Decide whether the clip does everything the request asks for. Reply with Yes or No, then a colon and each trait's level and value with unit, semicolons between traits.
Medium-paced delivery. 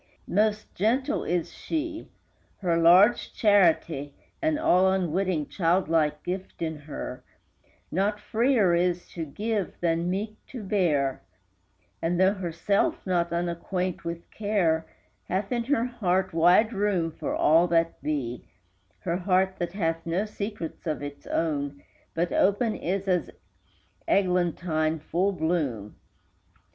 No: slow, 130 wpm